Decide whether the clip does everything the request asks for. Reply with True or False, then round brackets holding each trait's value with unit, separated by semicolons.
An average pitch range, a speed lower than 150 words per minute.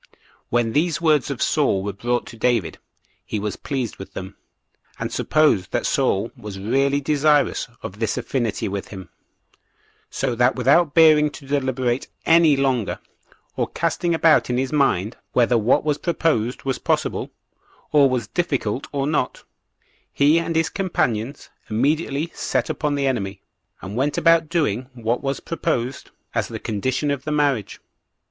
False (4.8 semitones; 155 wpm)